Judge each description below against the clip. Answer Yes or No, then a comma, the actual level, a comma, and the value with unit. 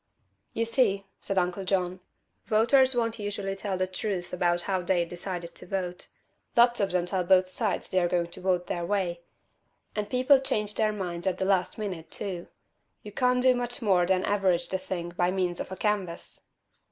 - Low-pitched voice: No, high, 190 Hz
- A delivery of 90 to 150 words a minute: No, average, 190 wpm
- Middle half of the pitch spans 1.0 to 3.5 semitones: Yes, average, 2.9 semitones